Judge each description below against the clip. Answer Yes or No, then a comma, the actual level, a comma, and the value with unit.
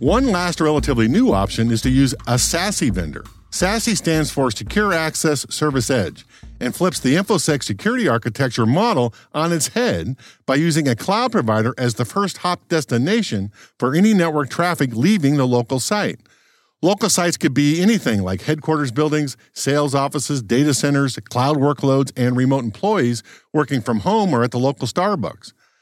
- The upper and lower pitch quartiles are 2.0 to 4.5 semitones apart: No, average, 5.2 semitones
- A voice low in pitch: No, medium, 145 Hz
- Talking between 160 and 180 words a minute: Yes, average, 165 wpm